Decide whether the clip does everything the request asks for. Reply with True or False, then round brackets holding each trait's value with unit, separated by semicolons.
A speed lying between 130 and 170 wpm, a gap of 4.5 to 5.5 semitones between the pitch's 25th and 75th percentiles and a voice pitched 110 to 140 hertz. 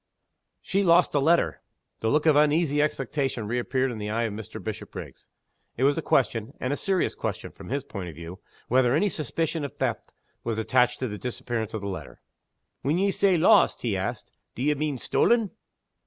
False (190 wpm; 5.2 semitones; 135 Hz)